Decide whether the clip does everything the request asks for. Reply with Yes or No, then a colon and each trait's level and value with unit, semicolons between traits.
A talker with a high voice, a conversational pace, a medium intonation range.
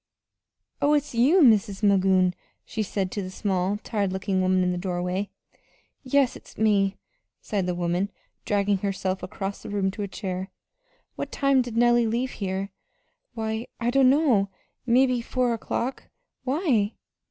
Yes: high, 205 Hz; average, 150 wpm; average, 4.0 semitones